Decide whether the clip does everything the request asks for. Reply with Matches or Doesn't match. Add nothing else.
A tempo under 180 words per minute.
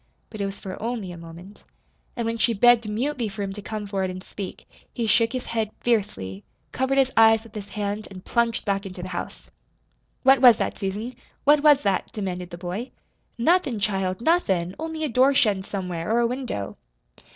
Doesn't match